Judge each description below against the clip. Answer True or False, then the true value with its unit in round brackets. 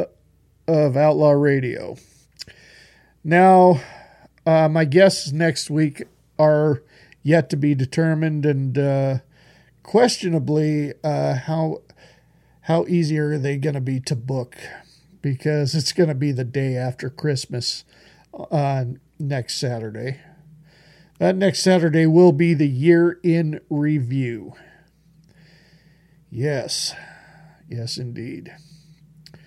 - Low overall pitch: False (155 Hz)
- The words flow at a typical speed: False (110 wpm)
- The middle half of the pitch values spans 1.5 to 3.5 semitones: True (2.9 semitones)